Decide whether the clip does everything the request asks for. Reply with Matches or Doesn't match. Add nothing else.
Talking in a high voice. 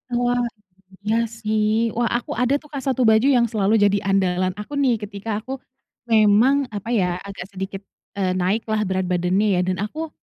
Matches